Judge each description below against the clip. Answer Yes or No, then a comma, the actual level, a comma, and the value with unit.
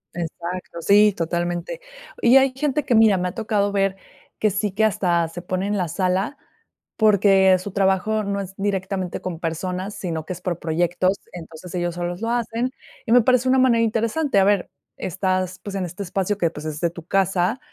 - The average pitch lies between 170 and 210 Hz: Yes, high, 190 Hz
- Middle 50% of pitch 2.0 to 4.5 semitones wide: Yes, average, 3.3 semitones